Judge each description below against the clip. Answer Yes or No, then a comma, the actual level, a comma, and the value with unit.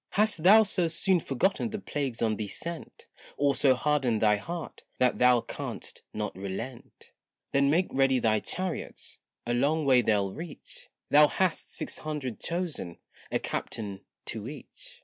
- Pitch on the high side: No, medium, 140 Hz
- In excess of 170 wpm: No, average, 155 wpm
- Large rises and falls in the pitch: Yes, wide, 6.8 semitones